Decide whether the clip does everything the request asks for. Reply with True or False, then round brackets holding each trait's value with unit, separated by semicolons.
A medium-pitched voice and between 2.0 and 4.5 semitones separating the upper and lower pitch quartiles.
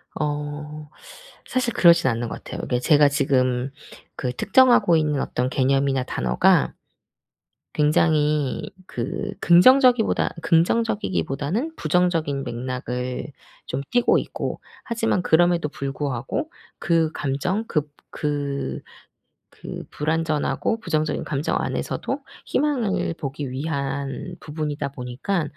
True (150 Hz; 4.2 semitones)